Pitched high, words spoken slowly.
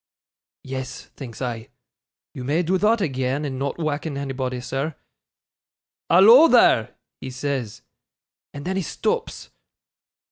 No: medium, 140 Hz; slow, 120 wpm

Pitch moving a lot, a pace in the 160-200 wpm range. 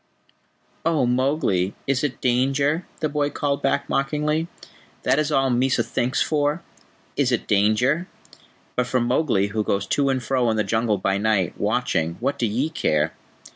No: average, 4.8 semitones; average, 165 wpm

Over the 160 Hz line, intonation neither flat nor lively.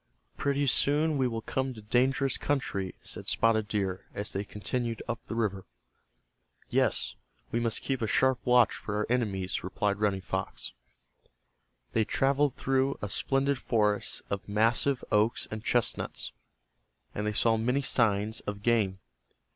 No: low, 115 Hz; average, 4.1 semitones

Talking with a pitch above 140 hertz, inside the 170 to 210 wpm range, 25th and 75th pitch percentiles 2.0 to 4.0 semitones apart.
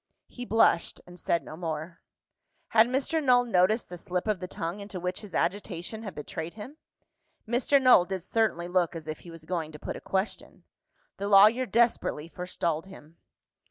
No: medium, 185 Hz; average, 180 wpm; average, 4.7 semitones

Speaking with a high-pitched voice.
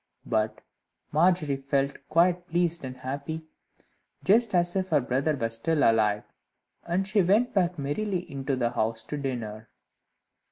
No: medium, 145 Hz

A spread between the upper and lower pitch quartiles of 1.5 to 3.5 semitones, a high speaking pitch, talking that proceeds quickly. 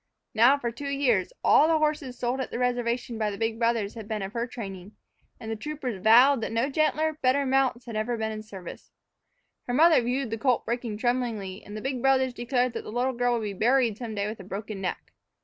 Yes: average, 3.2 semitones; high, 240 Hz; fast, 235 wpm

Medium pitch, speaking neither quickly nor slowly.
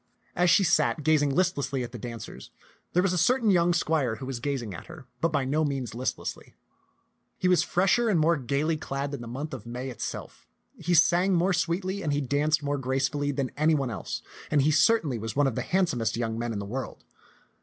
No: medium, 145 Hz; fast, 215 wpm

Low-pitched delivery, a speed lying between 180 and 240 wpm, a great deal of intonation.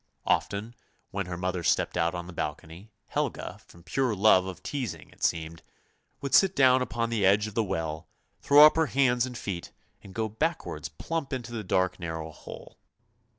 Yes: low, 100 Hz; average, 190 wpm; wide, 6.1 semitones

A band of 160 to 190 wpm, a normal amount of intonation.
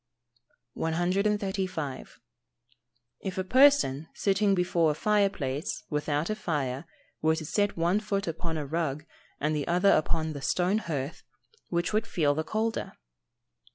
No: average, 140 wpm; average, 4.6 semitones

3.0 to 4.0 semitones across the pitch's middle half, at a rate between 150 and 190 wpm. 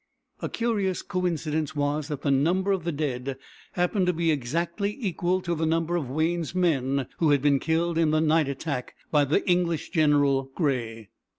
Yes: average, 3.4 semitones; average, 180 wpm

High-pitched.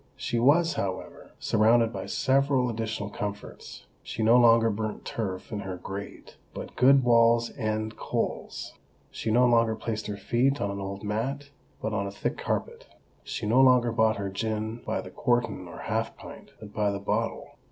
No: low, 110 Hz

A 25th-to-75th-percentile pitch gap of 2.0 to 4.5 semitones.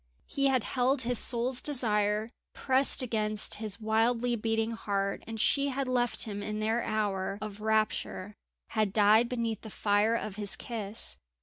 Yes: narrow, 2.5 semitones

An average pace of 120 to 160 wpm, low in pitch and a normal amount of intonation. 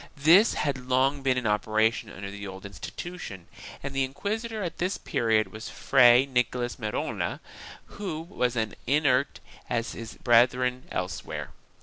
Yes: average, 145 wpm; low, 125 Hz; average, 4.2 semitones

